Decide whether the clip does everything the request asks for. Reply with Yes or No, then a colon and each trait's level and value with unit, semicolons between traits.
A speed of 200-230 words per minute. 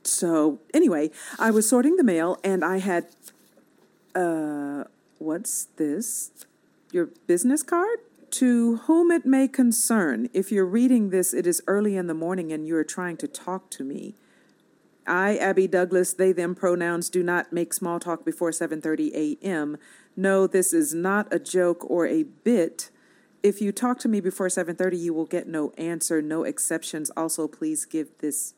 No: average, 170 wpm